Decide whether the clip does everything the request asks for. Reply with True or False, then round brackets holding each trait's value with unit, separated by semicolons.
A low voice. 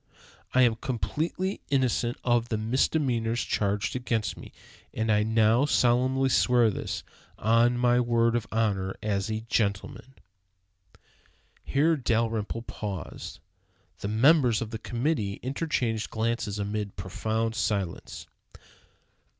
True (115 Hz)